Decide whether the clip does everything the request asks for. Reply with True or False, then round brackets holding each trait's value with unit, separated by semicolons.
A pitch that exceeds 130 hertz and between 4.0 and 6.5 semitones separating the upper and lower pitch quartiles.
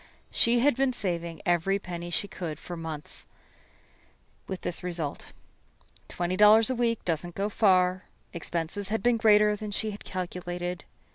False (185 Hz; 3.4 semitones)